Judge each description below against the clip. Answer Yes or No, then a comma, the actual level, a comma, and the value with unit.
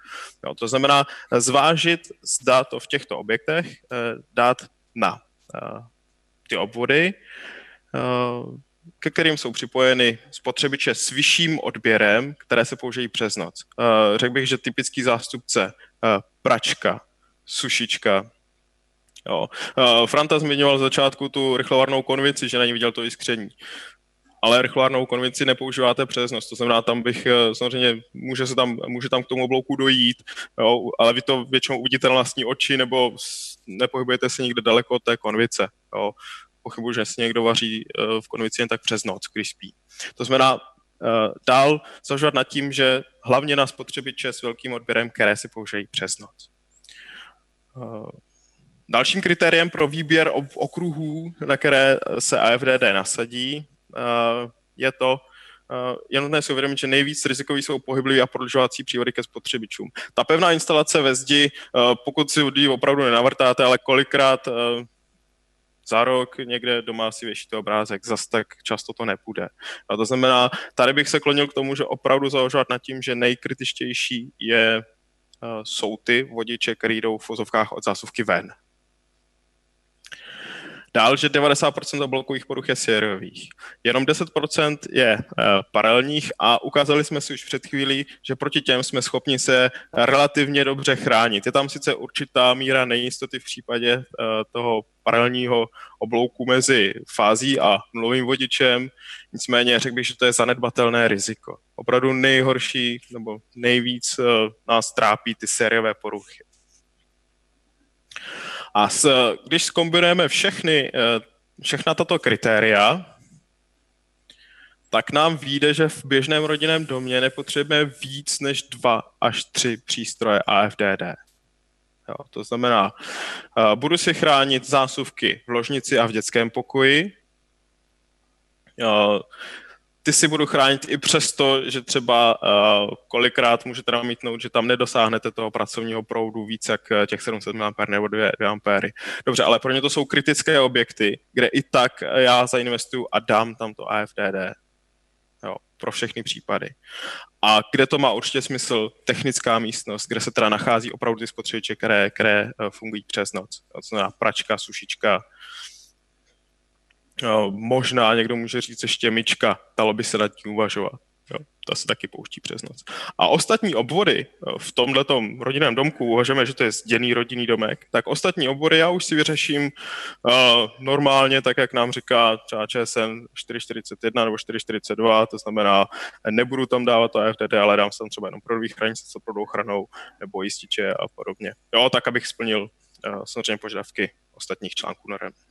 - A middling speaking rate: Yes, average, 145 wpm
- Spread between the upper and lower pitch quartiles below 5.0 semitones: Yes, average, 3.3 semitones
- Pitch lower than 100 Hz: No, low, 125 Hz